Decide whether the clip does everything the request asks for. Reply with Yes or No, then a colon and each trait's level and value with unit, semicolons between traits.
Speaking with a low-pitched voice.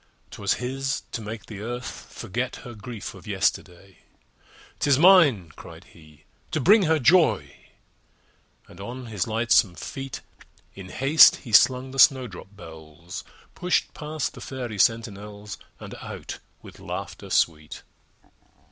Yes: low, 115 Hz